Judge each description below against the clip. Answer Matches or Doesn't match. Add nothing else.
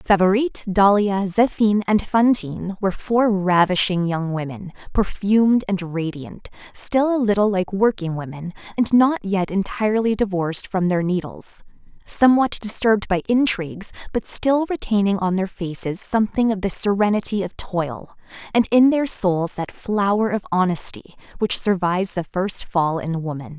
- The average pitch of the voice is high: Matches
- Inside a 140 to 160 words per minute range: Matches